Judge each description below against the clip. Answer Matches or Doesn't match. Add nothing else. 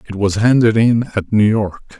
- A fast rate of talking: Matches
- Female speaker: Doesn't match